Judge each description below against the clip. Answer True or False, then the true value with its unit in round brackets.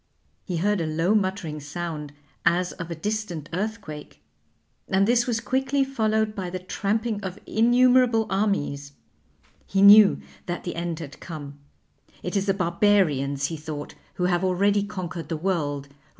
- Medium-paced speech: True (150 wpm)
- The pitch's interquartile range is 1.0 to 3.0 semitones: False (4.6 semitones)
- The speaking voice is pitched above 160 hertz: True (185 Hz)